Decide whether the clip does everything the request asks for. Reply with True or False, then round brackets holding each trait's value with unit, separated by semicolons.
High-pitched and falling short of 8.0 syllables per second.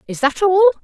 False (340 Hz; 8.3 syllables/s)